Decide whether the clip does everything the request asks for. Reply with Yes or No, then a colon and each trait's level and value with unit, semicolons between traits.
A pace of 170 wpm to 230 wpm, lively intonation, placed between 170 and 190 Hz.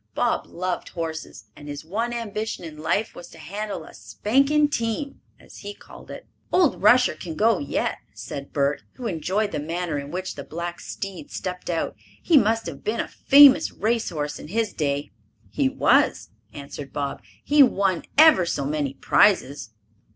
Yes: average, 175 wpm; wide, 7.2 semitones; medium, 185 Hz